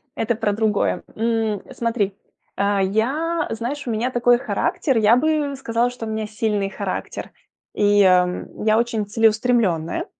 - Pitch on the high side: Yes, high, 225 Hz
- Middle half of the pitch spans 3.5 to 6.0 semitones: No, average, 2.9 semitones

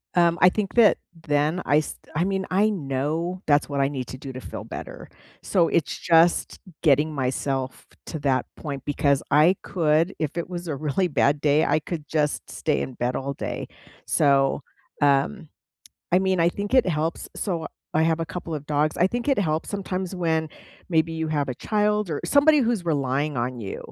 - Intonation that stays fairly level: No, average, 4.0 semitones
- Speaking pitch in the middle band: Yes, medium, 160 Hz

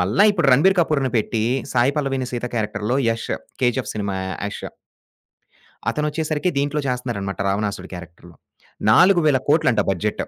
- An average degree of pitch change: No, wide, 6.0 semitones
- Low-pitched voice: Yes, low, 125 Hz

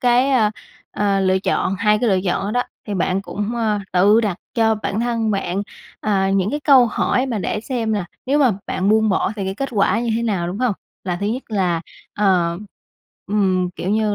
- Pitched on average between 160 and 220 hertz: Yes, high, 210 Hz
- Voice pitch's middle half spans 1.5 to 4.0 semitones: Yes, average, 3.1 semitones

